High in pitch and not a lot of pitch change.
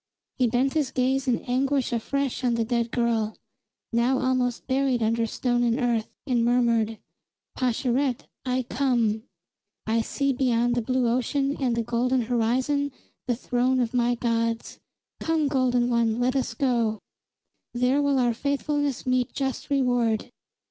Yes: high, 245 Hz; narrow, 2.1 semitones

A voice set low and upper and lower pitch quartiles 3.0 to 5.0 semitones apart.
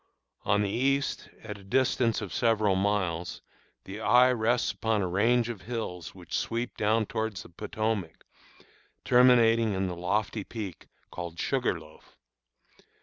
Yes: low, 110 Hz; average, 3.6 semitones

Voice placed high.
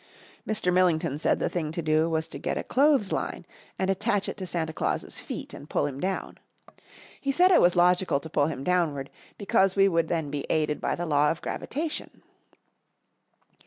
No: medium, 175 Hz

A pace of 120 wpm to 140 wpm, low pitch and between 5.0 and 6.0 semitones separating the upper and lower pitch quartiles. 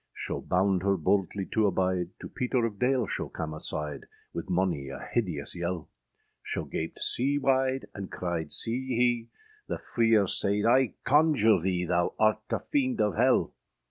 No: average, 165 wpm; low, 100 Hz; wide, 5.6 semitones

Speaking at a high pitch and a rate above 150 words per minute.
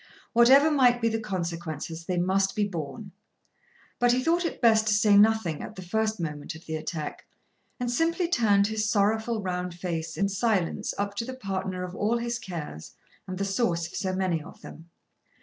Yes: high, 200 Hz; average, 190 wpm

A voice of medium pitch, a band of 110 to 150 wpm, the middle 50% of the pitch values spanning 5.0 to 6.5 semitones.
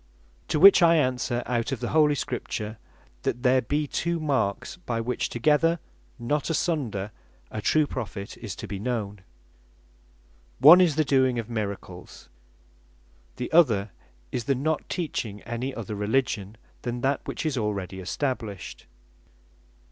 No: low, 125 Hz; average, 140 wpm; wide, 5.6 semitones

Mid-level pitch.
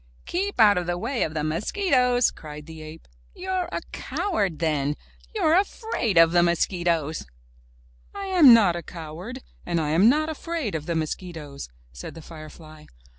Yes: medium, 175 Hz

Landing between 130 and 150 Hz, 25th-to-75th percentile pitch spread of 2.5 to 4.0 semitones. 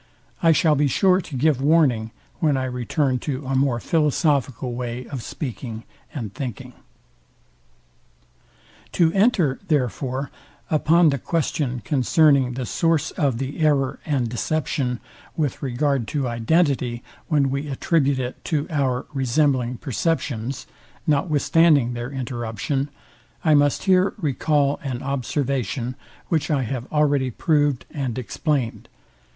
Yes: medium, 140 Hz; average, 3.3 semitones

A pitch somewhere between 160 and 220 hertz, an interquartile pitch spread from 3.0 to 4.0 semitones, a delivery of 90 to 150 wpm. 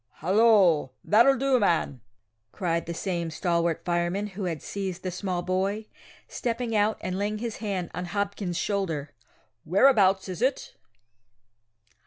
Yes: high, 190 Hz; average, 3.5 semitones; slow, 135 wpm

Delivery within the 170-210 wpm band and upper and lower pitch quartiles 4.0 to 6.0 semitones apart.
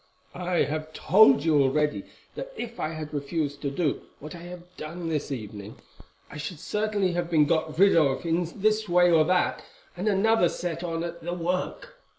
No: average, 185 wpm; average, 3.1 semitones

